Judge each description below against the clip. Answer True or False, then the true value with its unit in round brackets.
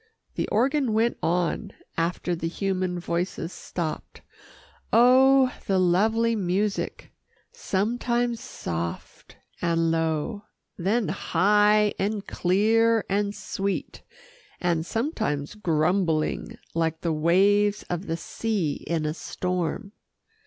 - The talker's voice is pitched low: False (195 Hz)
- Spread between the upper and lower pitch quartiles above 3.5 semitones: True (4.5 semitones)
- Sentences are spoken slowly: True (105 wpm)